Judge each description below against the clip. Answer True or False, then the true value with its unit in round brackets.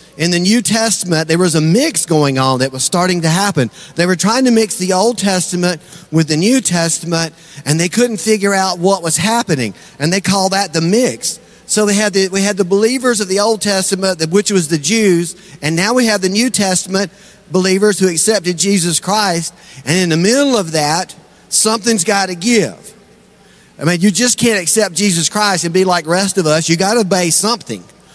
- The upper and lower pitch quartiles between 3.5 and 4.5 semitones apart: True (3.9 semitones)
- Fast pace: True (215 wpm)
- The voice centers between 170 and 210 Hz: True (190 Hz)